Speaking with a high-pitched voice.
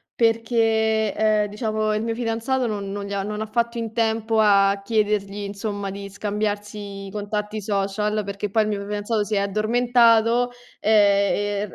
Yes: high, 210 Hz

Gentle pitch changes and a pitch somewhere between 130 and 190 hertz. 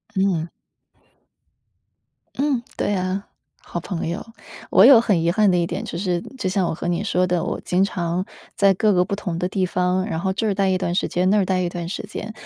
Yes: narrow, 2.3 semitones; medium, 185 Hz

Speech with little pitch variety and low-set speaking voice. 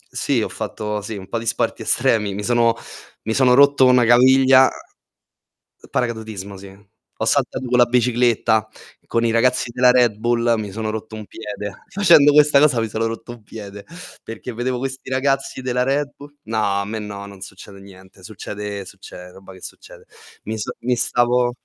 No: average, 3.3 semitones; low, 115 Hz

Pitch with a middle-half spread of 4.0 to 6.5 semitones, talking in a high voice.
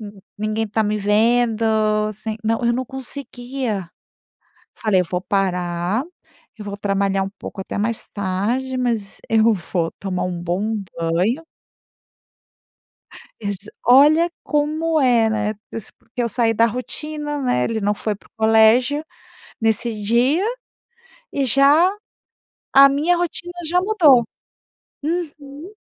Yes: average, 5.2 semitones; high, 225 Hz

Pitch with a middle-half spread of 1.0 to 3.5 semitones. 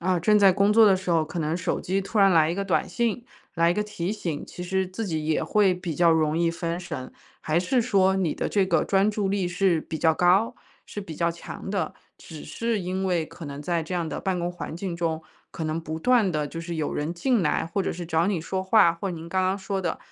Yes: average, 2.9 semitones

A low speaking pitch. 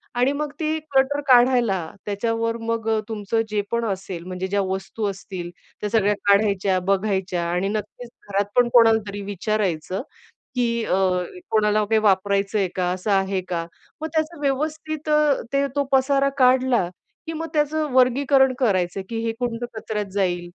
No: high, 220 Hz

